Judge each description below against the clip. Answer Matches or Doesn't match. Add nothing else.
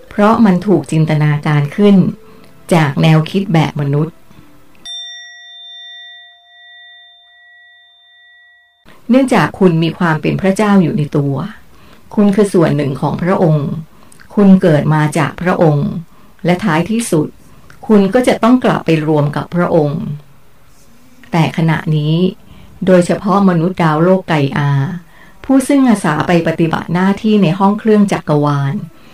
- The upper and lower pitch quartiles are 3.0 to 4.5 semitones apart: Doesn't match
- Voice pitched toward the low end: Doesn't match